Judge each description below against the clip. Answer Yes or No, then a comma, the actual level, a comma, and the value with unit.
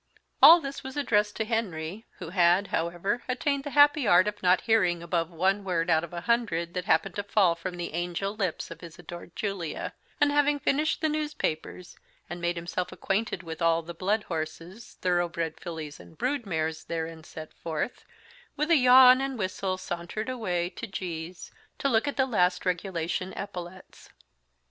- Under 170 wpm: No, average, 180 wpm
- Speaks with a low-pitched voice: No, medium, 185 Hz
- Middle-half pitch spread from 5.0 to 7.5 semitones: Yes, average, 5.3 semitones